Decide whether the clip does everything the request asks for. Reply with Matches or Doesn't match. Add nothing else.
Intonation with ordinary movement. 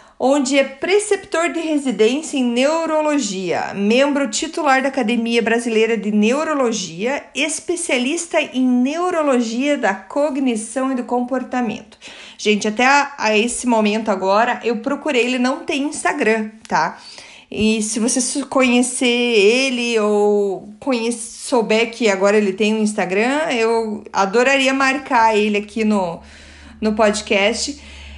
Matches